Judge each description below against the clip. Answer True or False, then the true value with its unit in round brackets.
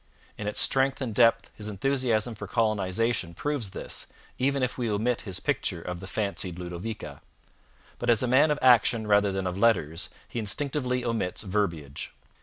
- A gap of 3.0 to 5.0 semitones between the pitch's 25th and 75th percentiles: True (4.5 semitones)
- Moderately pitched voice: False (110 Hz)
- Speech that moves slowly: False (170 wpm)